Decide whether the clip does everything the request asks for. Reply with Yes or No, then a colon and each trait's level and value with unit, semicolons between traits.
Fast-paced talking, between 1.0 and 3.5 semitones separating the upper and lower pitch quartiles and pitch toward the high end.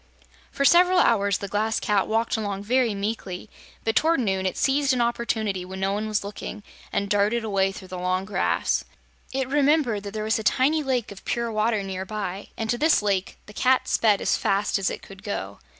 Yes: fast, 210 wpm; average, 3.2 semitones; high, 215 Hz